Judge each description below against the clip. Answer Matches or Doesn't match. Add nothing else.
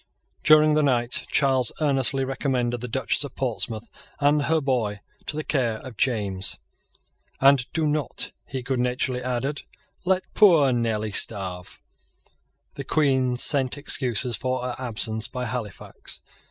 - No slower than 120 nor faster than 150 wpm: Matches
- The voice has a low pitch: Matches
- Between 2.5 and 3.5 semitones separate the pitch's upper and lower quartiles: Matches